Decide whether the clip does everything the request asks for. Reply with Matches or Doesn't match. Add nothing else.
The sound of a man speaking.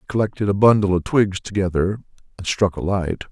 Matches